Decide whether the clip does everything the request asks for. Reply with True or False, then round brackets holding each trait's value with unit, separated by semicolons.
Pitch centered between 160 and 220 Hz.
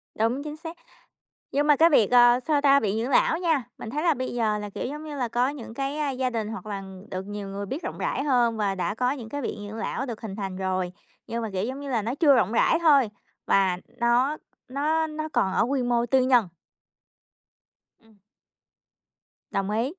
False (245 Hz)